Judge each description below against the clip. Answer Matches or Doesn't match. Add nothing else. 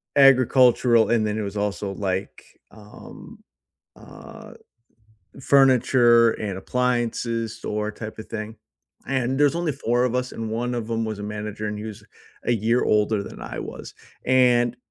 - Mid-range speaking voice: Doesn't match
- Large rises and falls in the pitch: Doesn't match